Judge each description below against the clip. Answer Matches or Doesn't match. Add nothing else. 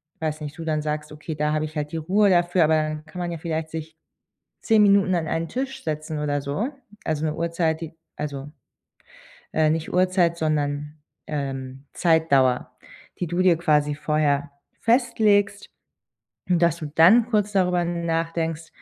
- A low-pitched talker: Doesn't match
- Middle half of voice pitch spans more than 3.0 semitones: Doesn't match